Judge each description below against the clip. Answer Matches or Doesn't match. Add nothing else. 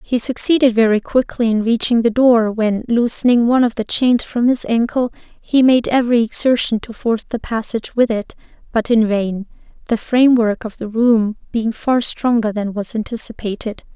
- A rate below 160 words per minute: Doesn't match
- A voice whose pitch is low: Doesn't match